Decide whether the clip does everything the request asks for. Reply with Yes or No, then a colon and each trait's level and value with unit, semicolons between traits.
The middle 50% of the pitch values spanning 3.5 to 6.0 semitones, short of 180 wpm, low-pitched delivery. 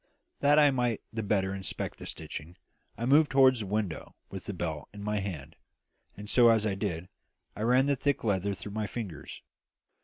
No: average, 4.3 semitones; average, 190 wpm; low, 105 Hz